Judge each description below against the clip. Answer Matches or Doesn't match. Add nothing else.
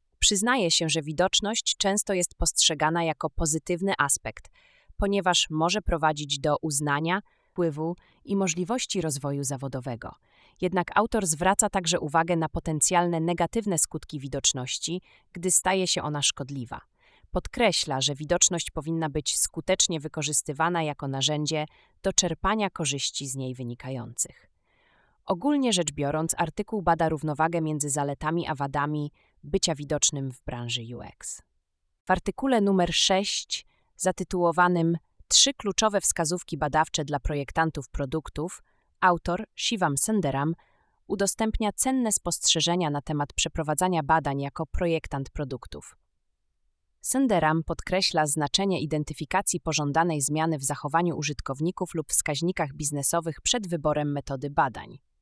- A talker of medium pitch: Matches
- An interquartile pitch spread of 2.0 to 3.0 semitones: Doesn't match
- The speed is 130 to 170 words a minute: Doesn't match